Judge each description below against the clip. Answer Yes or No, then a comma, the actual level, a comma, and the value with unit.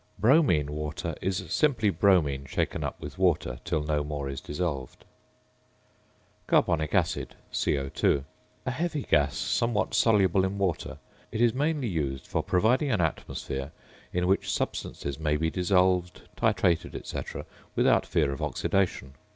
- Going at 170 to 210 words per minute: No, slow, 135 wpm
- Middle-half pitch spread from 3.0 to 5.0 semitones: No, wide, 5.5 semitones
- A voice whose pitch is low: Yes, very low, 90 Hz